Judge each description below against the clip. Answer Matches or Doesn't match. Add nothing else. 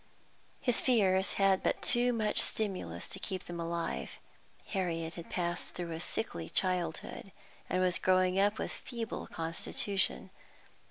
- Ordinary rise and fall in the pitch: Matches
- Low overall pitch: Doesn't match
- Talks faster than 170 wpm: Doesn't match